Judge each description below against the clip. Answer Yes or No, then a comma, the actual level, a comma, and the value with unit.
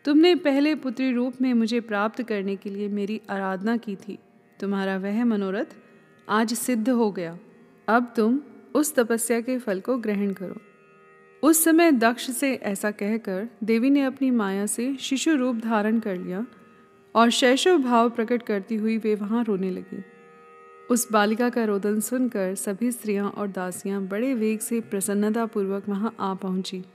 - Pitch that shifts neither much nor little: Yes, average, 3.3 semitones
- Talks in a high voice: Yes, high, 220 Hz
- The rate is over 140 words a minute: Yes, average, 160 wpm